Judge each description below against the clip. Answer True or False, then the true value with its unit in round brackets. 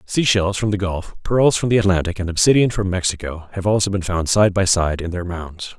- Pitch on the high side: False (95 Hz)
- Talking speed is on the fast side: True (240 wpm)